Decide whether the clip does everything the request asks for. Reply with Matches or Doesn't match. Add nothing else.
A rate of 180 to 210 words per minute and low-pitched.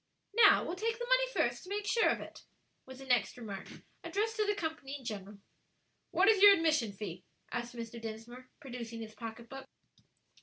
Doesn't match